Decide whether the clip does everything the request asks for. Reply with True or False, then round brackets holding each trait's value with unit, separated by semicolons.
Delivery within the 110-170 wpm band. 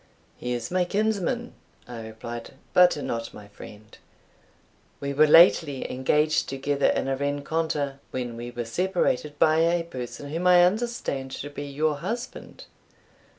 True (145 wpm)